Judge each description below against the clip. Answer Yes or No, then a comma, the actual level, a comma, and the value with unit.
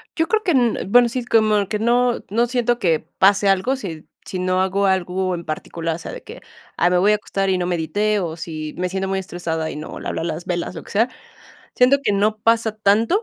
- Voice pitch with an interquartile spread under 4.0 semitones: No, average, 4.4 semitones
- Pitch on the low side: No, high, 195 Hz